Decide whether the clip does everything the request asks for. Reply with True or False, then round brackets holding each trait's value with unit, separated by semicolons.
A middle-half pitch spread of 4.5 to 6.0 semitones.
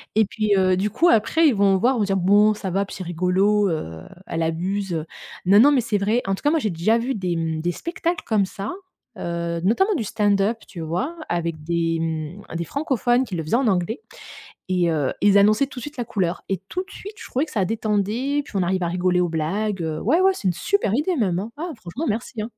True (5.4 semitones)